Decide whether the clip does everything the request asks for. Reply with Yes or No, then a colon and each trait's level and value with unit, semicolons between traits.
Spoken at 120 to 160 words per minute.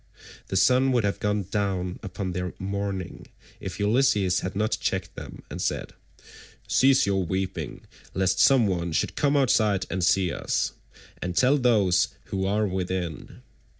Yes: average, 150 wpm